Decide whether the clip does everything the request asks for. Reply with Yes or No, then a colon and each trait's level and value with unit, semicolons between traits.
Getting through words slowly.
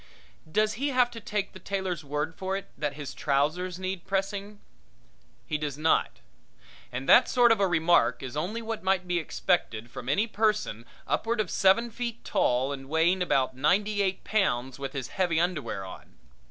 No: average, 180 wpm